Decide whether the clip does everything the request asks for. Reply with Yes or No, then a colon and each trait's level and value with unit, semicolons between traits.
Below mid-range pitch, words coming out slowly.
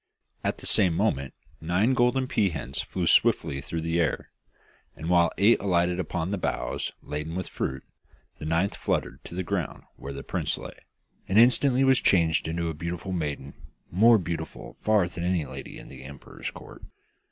No: very low, 85 Hz; average, 175 wpm